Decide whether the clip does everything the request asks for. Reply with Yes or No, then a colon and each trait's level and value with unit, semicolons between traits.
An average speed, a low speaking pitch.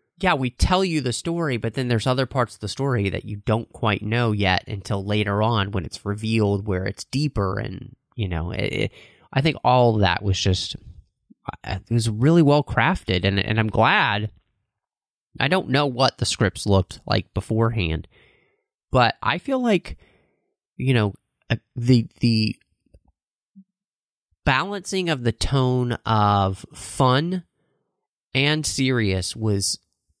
Yes: average, 150 wpm; low, 115 Hz